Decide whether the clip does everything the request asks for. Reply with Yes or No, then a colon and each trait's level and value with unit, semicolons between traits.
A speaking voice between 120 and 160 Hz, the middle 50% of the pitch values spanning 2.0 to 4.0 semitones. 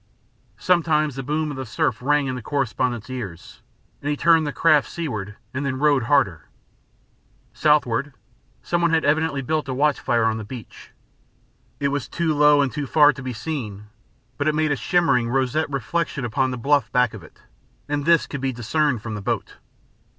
Yes: medium, 140 Hz; average, 3.7 semitones